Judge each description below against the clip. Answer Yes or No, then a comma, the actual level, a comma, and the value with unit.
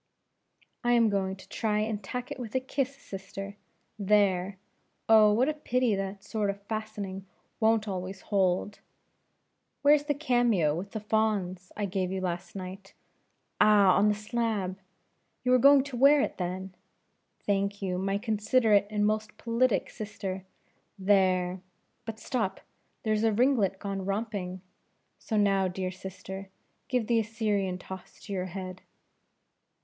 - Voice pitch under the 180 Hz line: No, high, 205 Hz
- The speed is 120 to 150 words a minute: Yes, average, 145 wpm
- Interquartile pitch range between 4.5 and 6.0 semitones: No, average, 2.8 semitones